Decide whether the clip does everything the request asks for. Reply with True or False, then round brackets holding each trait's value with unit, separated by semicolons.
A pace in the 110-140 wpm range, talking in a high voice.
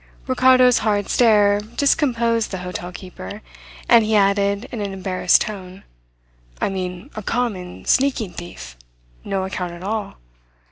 True (135 wpm; 205 Hz)